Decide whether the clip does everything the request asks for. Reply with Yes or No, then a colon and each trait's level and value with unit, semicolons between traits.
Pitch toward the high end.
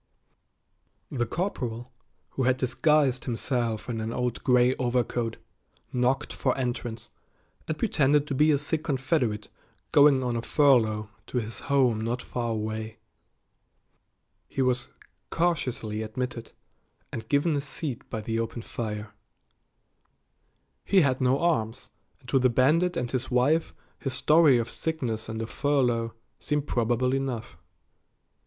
No: low, 125 Hz